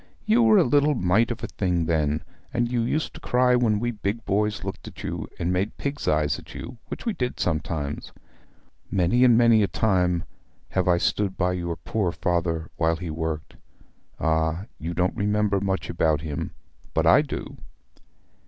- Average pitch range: No, wide, 5.9 semitones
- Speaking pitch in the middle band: No, very low, 95 Hz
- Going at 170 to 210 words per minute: Yes, average, 180 wpm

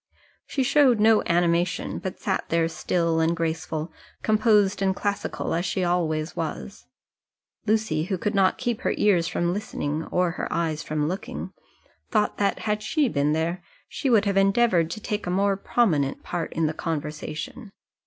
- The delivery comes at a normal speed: Yes, average, 165 wpm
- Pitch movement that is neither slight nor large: Yes, average, 4.3 semitones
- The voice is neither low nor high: Yes, medium, 180 Hz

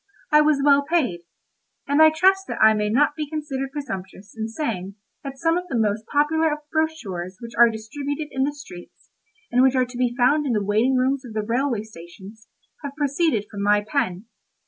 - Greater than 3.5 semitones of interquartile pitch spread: Yes, wide, 5.5 semitones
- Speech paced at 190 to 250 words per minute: Yes, fast, 205 wpm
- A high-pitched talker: Yes, very high, 260 Hz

